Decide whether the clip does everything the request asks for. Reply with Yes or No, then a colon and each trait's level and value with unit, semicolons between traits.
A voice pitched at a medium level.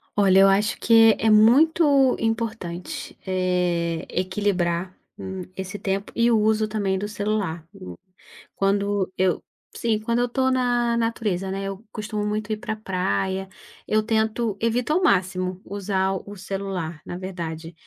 No: high, 200 Hz